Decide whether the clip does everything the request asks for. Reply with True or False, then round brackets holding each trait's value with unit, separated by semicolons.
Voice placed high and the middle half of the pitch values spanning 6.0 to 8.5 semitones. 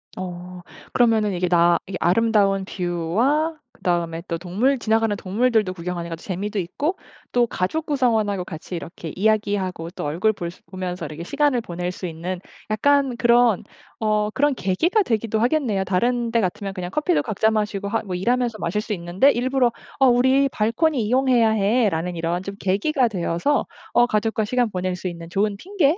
False (210 Hz; 5.2 semitones)